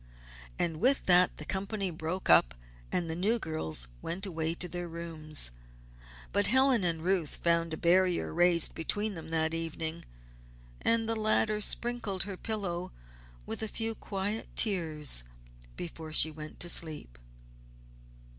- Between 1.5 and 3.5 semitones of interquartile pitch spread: No, average, 4.1 semitones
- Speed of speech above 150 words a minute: No, average, 145 wpm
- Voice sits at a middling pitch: Yes, medium, 175 Hz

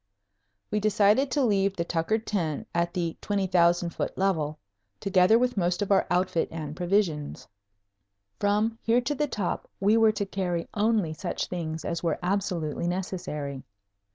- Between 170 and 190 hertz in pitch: Yes, medium, 185 Hz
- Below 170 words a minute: Yes, average, 155 wpm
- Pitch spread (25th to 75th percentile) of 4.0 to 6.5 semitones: No, average, 3.6 semitones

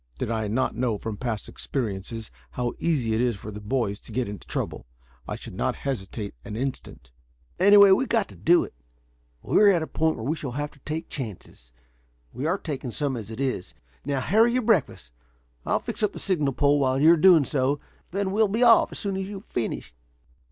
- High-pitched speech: No, low, 135 Hz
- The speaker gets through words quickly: Yes, fast, 215 wpm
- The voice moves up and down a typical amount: No, wide, 7.7 semitones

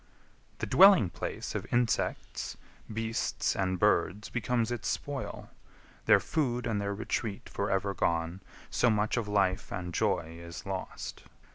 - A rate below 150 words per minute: Yes, average, 140 wpm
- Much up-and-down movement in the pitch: No, average, 3.8 semitones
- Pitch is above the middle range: No, low, 105 Hz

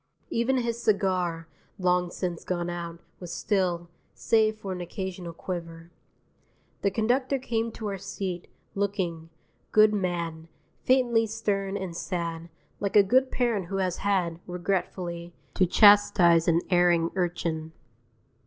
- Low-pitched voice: No, medium, 185 Hz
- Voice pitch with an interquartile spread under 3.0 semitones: No, average, 3.3 semitones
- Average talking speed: No, slow, 130 wpm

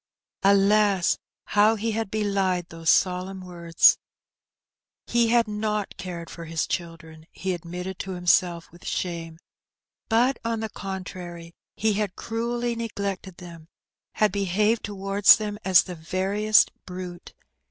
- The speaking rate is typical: No, slow, 130 wpm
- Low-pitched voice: No, high, 190 Hz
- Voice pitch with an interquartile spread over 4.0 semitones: No, average, 3.3 semitones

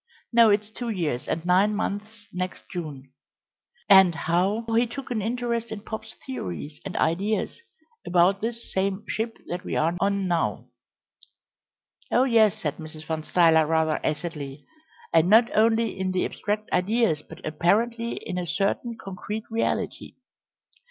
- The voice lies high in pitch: Yes, high, 195 Hz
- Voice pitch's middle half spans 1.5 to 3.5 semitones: No, average, 5.0 semitones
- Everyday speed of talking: Yes, average, 150 wpm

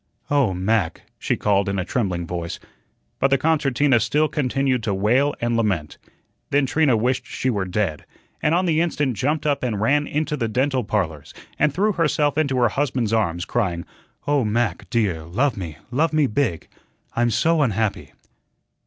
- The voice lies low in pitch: Yes, low, 125 Hz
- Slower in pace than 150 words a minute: No, average, 170 wpm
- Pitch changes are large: Yes, wide, 6.0 semitones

